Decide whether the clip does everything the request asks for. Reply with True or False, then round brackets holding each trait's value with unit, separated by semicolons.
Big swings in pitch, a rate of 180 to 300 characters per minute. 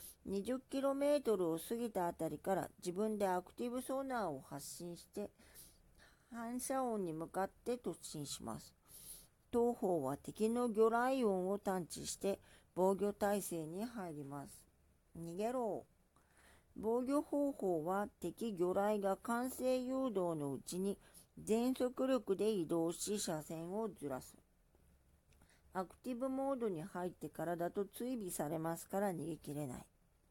True (6.1 semitones; 250 characters per minute)